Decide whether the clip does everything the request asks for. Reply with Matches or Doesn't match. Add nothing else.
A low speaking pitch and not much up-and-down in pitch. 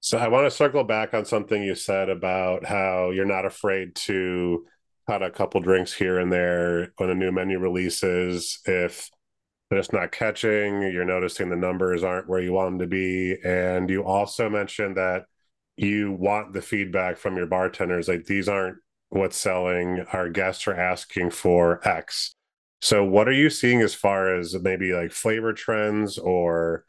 Matches